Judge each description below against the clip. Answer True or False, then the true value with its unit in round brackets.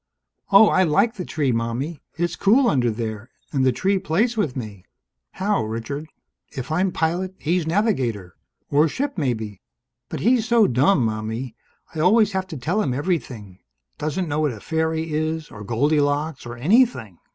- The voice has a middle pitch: True (155 Hz)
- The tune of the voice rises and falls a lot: True (7.6 semitones)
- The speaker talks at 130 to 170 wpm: True (165 wpm)